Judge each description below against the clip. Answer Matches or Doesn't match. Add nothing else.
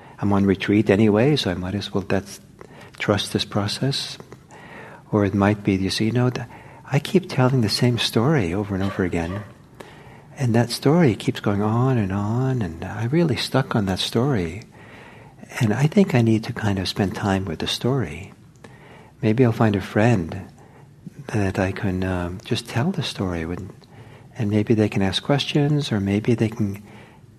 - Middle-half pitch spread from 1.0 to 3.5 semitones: Doesn't match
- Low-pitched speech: Matches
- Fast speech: Doesn't match